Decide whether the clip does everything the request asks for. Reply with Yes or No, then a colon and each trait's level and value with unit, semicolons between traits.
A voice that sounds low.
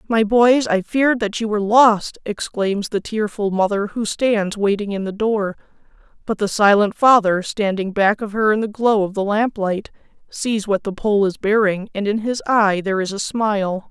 No: high, 210 Hz